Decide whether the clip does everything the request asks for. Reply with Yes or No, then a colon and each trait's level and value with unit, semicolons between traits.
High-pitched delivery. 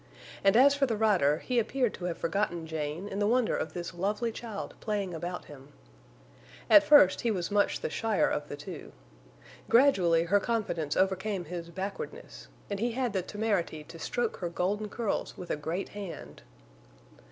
Yes: high, 195 Hz